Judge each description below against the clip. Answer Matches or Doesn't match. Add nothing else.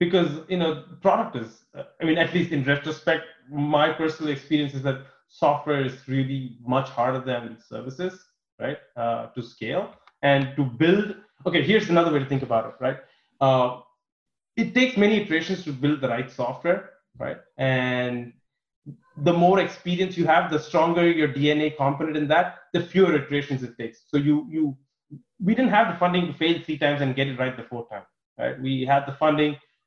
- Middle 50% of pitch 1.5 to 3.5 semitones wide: Doesn't match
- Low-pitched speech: Doesn't match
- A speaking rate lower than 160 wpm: Doesn't match